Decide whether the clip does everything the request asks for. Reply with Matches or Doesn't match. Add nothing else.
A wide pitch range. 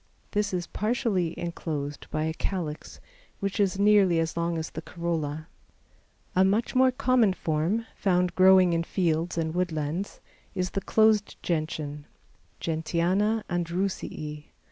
Doesn't match